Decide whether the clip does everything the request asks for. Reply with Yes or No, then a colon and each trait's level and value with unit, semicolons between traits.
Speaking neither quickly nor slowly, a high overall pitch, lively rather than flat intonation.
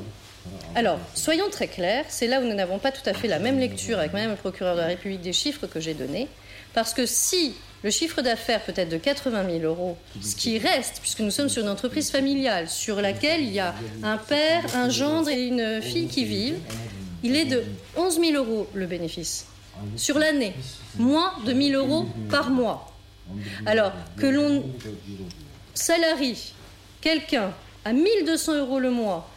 Yes: average, 190 wpm; high, 225 Hz; wide, 8.9 semitones